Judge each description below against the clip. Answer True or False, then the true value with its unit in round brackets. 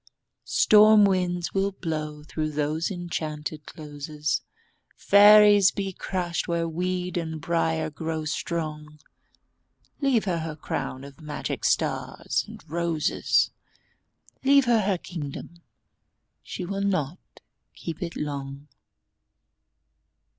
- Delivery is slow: True (105 wpm)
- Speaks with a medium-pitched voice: True (165 Hz)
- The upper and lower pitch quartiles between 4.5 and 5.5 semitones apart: False (3.7 semitones)